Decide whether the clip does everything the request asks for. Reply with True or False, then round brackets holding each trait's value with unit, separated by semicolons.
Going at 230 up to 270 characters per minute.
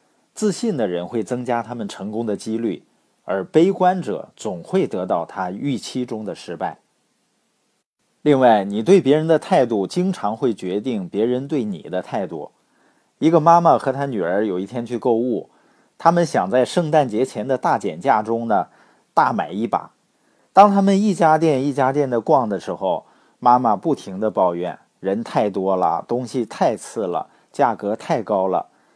True (240 characters per minute)